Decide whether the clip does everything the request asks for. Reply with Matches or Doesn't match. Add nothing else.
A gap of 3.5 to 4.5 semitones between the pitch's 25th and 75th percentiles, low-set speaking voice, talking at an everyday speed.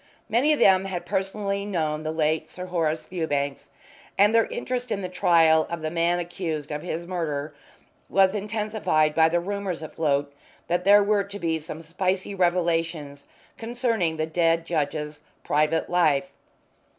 Doesn't match